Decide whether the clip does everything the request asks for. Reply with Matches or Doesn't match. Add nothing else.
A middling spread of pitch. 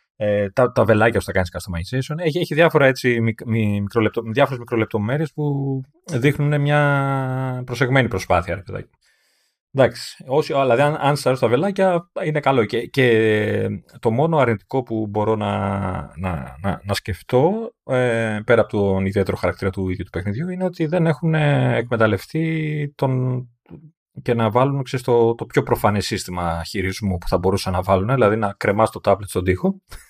Doesn't match